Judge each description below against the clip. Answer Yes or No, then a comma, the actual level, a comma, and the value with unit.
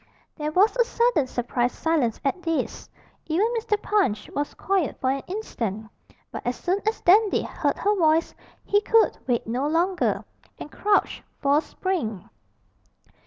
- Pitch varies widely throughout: Yes, wide, 7.6 semitones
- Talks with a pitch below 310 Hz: No, very high, 330 Hz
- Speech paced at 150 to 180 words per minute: Yes, average, 155 wpm